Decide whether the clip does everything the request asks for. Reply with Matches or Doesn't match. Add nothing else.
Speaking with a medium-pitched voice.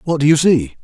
Matches